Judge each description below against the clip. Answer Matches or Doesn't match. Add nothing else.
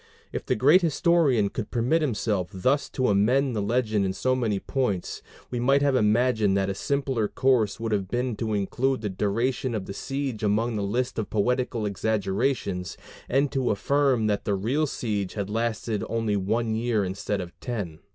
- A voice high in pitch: Doesn't match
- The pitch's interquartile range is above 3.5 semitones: Matches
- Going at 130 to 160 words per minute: Doesn't match